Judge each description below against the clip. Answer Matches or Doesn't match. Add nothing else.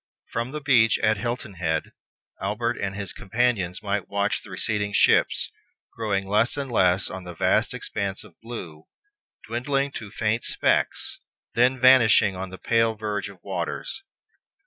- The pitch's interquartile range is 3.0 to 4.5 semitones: Matches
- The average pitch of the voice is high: Doesn't match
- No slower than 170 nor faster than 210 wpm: Doesn't match